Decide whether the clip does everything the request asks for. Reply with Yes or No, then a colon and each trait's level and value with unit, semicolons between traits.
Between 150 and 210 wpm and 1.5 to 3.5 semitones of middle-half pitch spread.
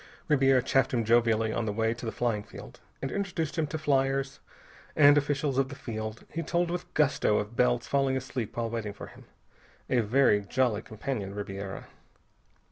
No: average, 180 wpm; average, 4.0 semitones